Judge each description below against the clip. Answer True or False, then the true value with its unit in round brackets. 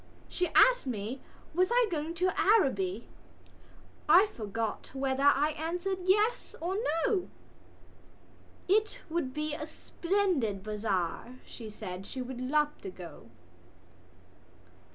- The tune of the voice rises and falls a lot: True (8.5 semitones)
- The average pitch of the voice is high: True (295 Hz)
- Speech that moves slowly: True (115 wpm)